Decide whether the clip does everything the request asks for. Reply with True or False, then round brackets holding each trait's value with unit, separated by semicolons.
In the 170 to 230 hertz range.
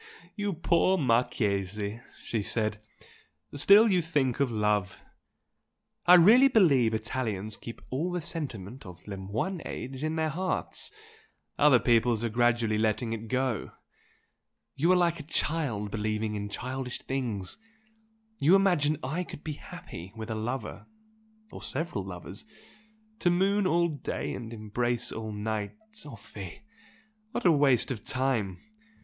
False (125 Hz)